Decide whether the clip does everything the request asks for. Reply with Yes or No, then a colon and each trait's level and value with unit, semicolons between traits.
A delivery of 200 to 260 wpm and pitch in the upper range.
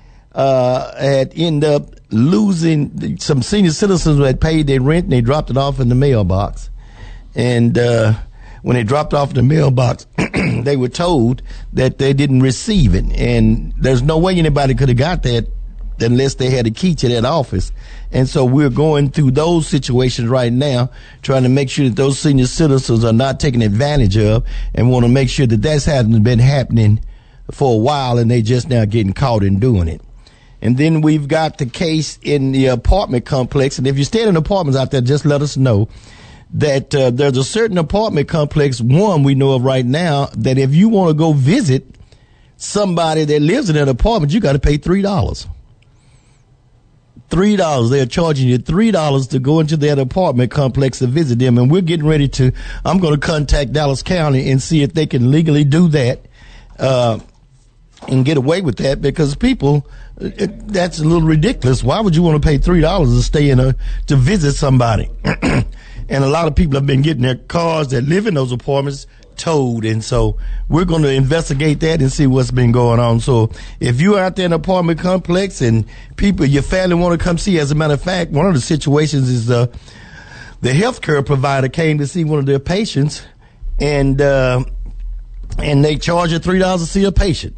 No: fast, 205 wpm; medium, 140 Hz